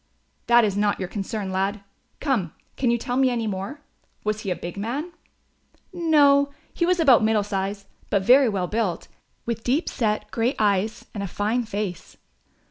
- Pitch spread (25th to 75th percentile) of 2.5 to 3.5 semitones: No, average, 3.9 semitones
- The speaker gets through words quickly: No, average, 175 wpm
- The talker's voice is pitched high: Yes, high, 215 Hz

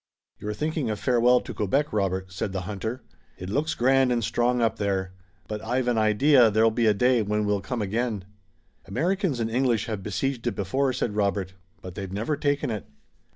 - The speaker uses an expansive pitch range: No, average, 3.8 semitones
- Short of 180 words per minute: No, average, 195 wpm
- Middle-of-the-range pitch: No, low, 110 Hz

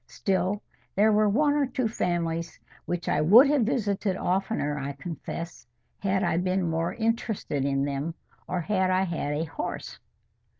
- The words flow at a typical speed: Yes, average, 160 wpm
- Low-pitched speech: No, medium, 185 Hz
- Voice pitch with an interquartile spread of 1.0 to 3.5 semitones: No, average, 4.6 semitones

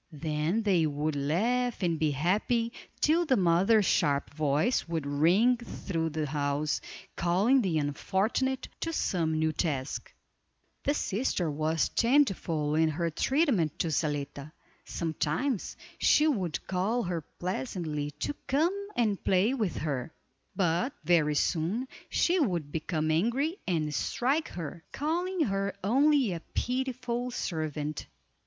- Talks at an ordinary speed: No, slow, 130 wpm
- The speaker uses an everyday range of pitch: No, wide, 7.9 semitones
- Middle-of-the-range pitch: Yes, medium, 175 Hz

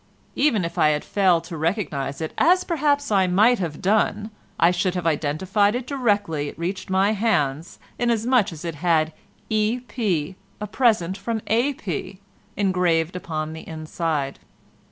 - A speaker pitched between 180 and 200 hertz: Yes, medium, 185 Hz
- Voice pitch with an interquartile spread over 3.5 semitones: Yes, average, 5.1 semitones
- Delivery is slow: No, average, 155 wpm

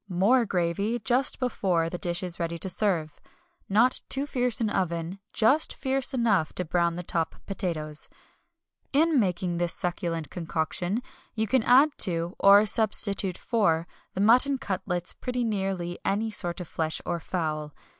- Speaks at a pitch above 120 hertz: Yes, high, 190 Hz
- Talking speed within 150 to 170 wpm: Yes, average, 155 wpm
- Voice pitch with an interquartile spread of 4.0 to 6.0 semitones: Yes, average, 5.0 semitones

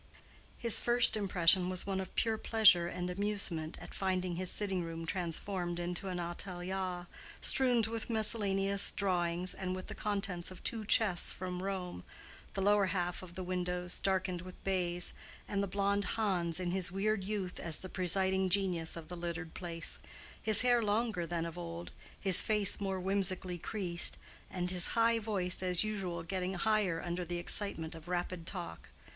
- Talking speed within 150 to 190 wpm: Yes, average, 165 wpm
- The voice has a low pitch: No, medium, 185 Hz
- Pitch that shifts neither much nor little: No, narrow, 2.3 semitones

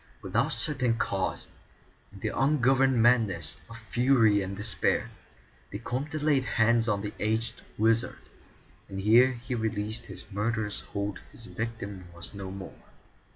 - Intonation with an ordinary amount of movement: Yes, average, 3.3 semitones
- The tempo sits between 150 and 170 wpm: No, average, 140 wpm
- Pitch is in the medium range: No, low, 110 Hz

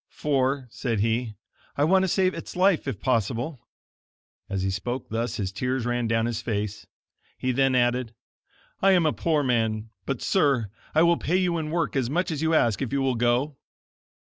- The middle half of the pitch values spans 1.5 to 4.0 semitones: No, average, 5.1 semitones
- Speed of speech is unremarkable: Yes, average, 190 wpm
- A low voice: Yes, low, 130 Hz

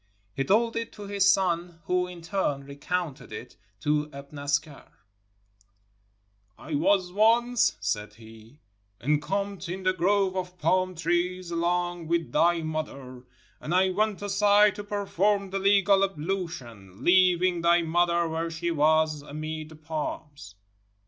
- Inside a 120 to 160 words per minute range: Yes, average, 140 wpm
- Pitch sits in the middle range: Yes, medium, 170 Hz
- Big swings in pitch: No, average, 4.3 semitones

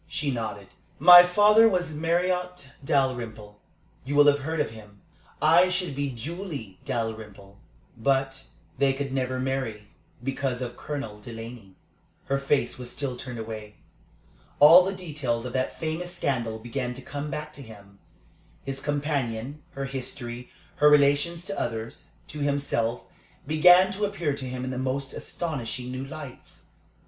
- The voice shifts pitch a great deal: No, average, 4.2 semitones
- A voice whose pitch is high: No, low, 135 Hz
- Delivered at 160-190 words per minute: No, average, 150 wpm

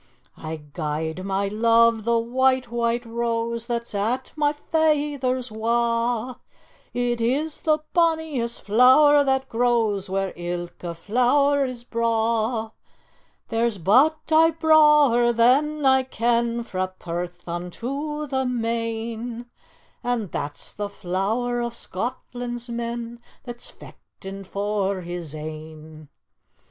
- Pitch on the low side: No, high, 235 Hz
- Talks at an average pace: No, slow, 110 wpm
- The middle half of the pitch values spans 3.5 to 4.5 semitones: Yes, average, 4.1 semitones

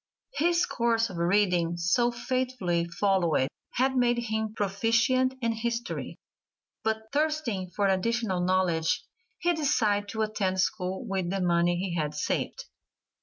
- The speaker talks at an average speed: No, slow, 130 wpm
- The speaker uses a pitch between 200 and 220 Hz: Yes, high, 210 Hz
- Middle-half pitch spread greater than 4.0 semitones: Yes, average, 4.8 semitones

